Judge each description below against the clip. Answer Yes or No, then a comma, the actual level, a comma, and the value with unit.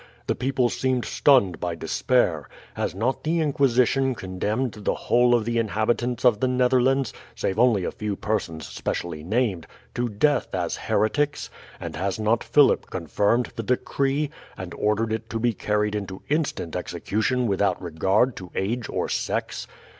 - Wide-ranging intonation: No, average, 4.4 semitones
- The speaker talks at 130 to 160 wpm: Yes, average, 155 wpm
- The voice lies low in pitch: Yes, low, 115 Hz